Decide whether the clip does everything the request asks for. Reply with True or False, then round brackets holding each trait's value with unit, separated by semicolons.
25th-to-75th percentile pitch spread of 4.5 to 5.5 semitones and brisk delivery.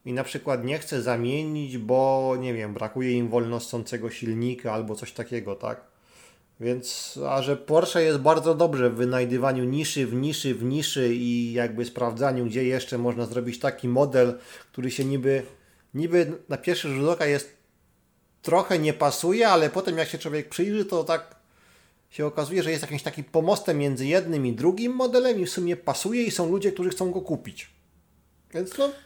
True (5.1 semitones; 180 wpm)